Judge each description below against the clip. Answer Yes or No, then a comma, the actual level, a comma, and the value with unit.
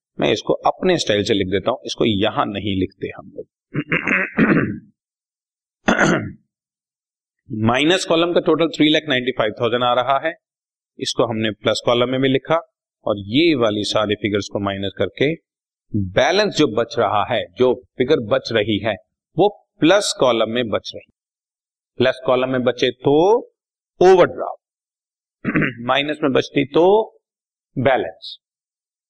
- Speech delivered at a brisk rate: No, average, 140 wpm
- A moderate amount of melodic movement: No, wide, 6.3 semitones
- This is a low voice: Yes, low, 130 Hz